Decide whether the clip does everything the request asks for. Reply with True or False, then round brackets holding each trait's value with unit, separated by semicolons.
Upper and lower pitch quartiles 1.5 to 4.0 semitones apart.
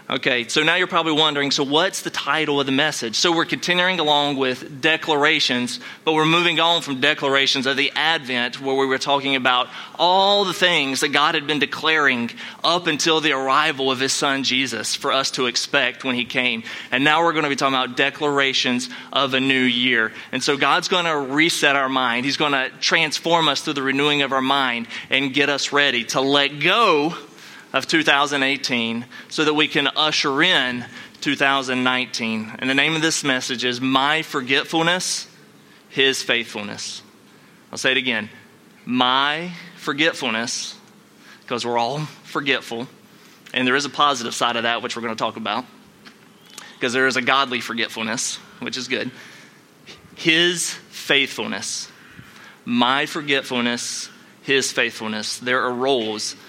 True (3.7 semitones)